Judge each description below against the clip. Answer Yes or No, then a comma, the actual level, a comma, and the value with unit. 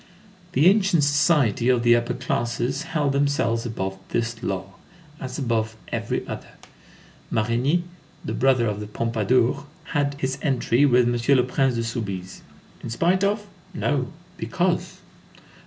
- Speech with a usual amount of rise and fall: Yes, average, 3.6 semitones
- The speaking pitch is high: No, low, 125 Hz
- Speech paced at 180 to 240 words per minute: No, average, 140 wpm